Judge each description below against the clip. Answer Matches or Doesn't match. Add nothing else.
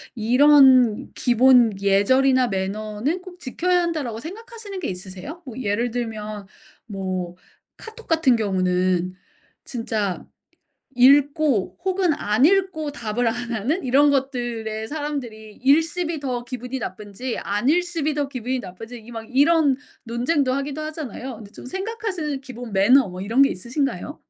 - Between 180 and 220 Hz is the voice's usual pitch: Doesn't match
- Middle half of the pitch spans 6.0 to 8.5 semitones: Doesn't match